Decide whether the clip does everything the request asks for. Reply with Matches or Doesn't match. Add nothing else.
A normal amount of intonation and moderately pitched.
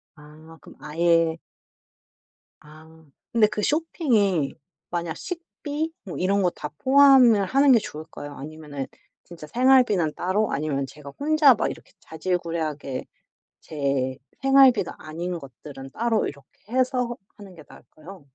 Doesn't match